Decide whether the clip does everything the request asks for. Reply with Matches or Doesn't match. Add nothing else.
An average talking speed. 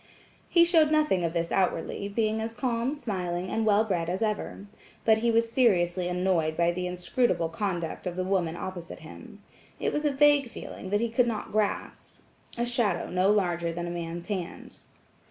Matches